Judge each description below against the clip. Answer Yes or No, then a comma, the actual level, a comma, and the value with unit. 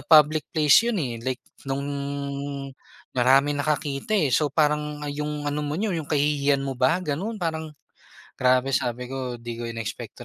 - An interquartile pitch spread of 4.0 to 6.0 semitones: No, average, 2.7 semitones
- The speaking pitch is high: No, medium, 145 Hz